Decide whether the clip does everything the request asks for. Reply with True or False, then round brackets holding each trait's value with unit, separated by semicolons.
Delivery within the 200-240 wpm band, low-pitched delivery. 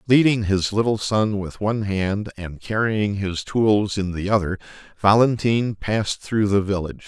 False (160 wpm; 105 Hz)